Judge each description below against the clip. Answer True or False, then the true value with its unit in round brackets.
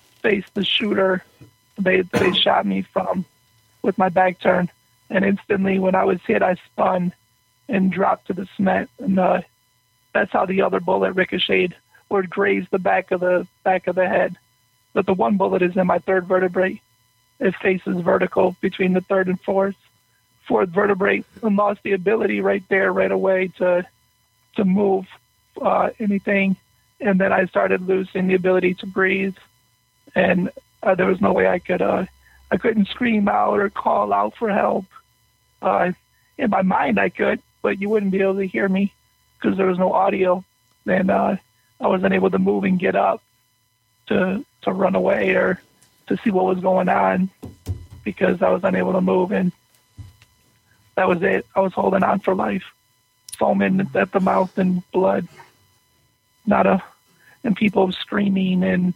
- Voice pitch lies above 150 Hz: True (185 Hz)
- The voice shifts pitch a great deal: True (7.6 semitones)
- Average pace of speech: True (175 wpm)